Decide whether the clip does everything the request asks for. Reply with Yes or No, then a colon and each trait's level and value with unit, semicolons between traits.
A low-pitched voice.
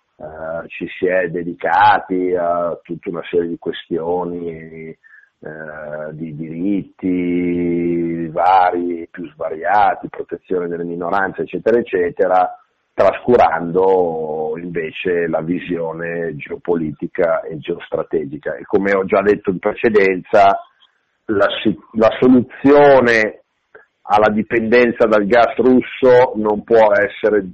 Yes: very low, 90 Hz